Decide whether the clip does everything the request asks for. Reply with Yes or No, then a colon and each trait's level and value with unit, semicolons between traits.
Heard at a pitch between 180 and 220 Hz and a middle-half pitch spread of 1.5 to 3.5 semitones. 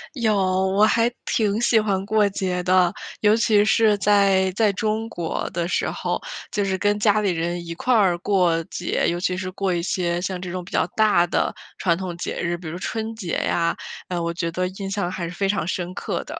Yes: high, 190 Hz; average, 3.0 semitones